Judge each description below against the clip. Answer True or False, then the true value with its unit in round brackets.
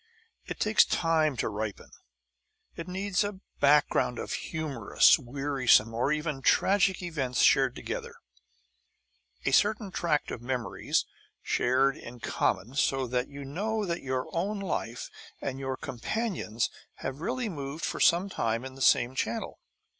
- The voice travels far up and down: True (6.2 semitones)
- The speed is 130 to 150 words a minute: True (140 wpm)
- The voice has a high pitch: False (140 Hz)